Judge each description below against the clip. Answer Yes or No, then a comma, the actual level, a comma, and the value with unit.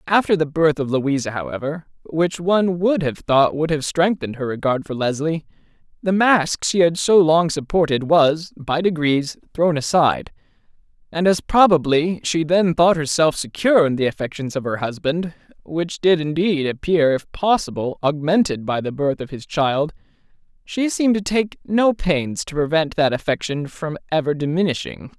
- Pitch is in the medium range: Yes, medium, 160 Hz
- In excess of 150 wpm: Yes, average, 165 wpm